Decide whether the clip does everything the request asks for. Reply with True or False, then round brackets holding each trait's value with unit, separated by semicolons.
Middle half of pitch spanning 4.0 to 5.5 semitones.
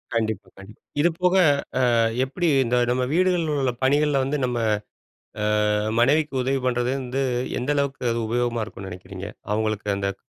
True (4.6 semitones)